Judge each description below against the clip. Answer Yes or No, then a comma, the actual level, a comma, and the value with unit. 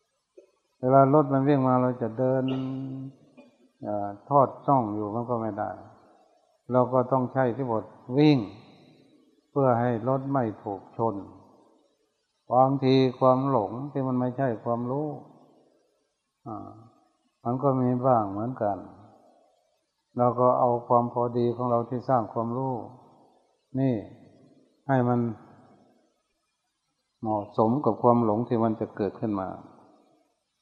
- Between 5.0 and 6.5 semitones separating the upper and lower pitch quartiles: No, narrow, 2.5 semitones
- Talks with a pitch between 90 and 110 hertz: No, low, 125 Hz